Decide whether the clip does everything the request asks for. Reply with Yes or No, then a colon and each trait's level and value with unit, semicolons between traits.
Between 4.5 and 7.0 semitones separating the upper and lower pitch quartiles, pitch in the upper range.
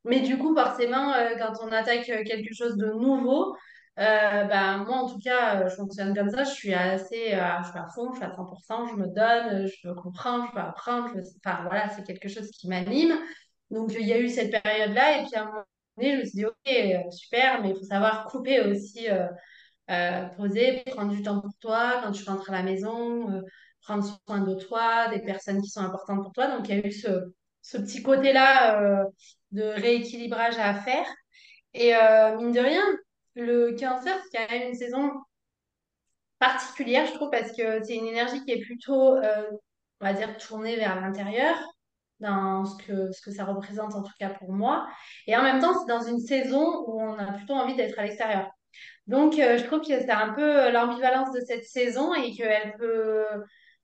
No: average, 3.9 semitones; high, 225 Hz